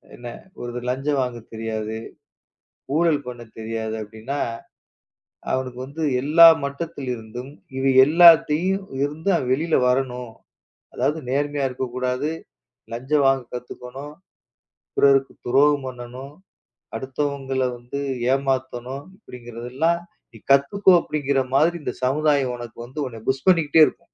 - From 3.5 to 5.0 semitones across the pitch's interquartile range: No, average, 3.0 semitones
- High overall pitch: No, low, 135 Hz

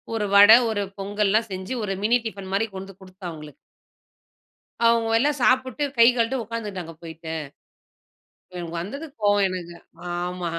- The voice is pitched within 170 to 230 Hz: Yes, high, 200 Hz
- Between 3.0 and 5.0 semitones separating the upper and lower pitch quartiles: Yes, average, 3.9 semitones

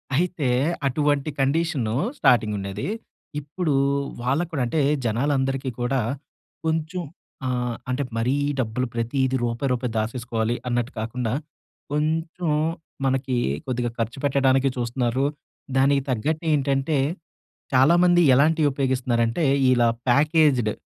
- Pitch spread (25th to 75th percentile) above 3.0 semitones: Yes, average, 3.7 semitones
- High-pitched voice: No, low, 135 Hz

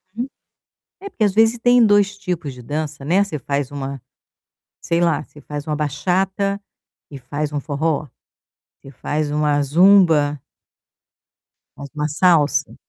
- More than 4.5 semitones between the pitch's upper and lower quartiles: Yes, average, 4.9 semitones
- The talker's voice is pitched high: No, medium, 150 Hz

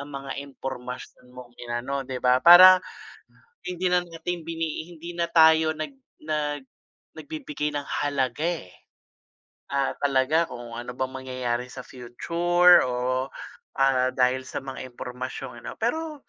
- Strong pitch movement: No, average, 4.5 semitones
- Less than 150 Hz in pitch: Yes, medium, 140 Hz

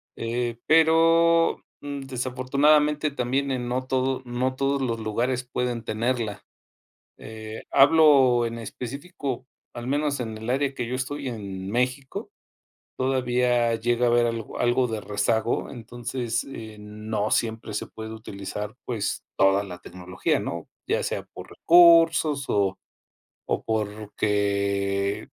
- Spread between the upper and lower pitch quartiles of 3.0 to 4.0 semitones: Yes, average, 3.5 semitones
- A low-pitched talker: Yes, low, 120 Hz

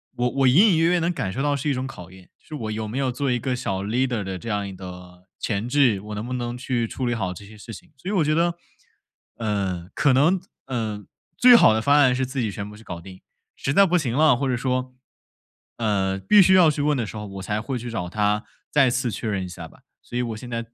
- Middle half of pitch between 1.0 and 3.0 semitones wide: No, average, 4.8 semitones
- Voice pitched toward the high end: No, low, 120 Hz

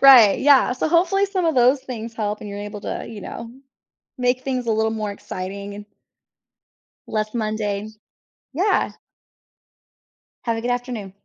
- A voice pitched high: Yes, high, 230 Hz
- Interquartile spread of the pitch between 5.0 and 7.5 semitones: No, average, 3.7 semitones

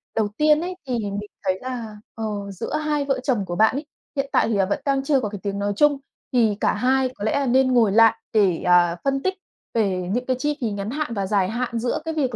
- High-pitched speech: Yes, high, 230 Hz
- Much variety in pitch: No, average, 4.9 semitones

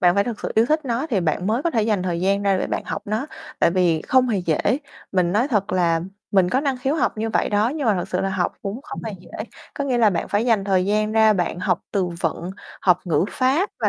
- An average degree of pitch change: Yes, average, 4.5 semitones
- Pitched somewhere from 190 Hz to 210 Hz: Yes, high, 205 Hz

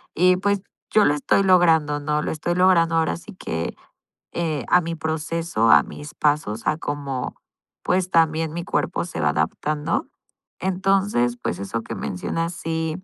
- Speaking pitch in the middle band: Yes, medium, 160 Hz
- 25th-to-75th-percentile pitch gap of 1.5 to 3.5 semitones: Yes, average, 3.2 semitones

